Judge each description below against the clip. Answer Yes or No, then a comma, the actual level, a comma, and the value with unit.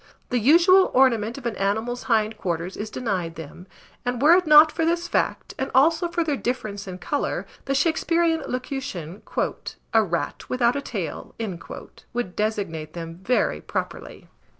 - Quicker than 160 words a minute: No, average, 155 wpm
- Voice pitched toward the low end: No, high, 245 Hz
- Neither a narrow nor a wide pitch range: No, wide, 7.0 semitones